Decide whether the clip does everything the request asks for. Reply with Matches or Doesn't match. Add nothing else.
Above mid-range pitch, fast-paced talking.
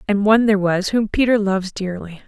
Matches